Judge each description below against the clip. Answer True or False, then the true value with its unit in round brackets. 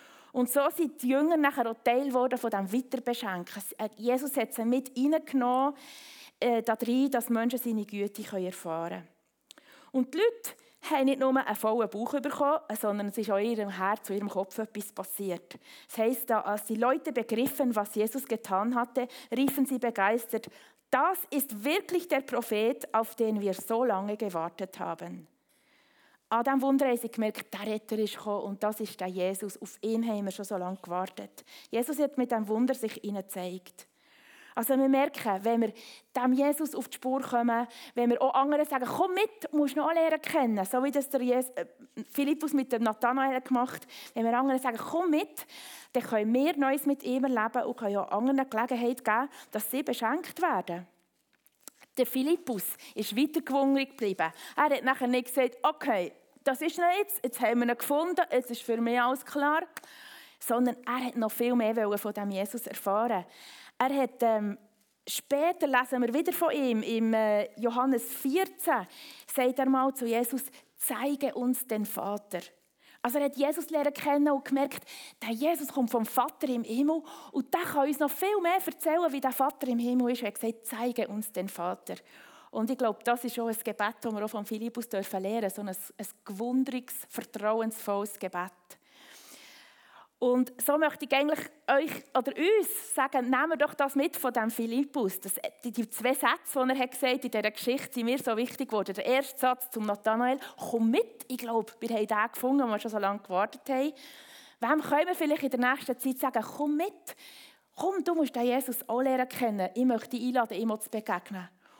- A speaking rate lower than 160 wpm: False (190 wpm)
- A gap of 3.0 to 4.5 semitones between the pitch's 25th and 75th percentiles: True (4.1 semitones)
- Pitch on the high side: True (250 Hz)